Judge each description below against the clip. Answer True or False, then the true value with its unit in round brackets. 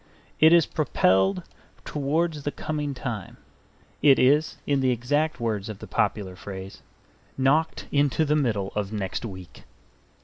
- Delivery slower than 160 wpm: True (140 wpm)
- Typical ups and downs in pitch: False (6.7 semitones)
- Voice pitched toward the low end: True (130 Hz)